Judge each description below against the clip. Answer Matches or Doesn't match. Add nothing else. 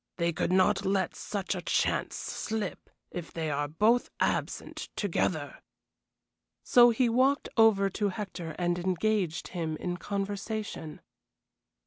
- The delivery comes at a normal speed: Doesn't match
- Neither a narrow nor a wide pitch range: Matches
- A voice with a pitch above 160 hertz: Matches